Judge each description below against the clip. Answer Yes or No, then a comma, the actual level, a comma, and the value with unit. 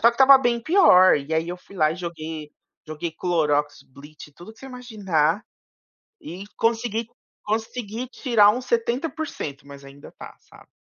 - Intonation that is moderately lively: No, wide, 7.2 semitones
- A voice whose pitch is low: No, high, 195 Hz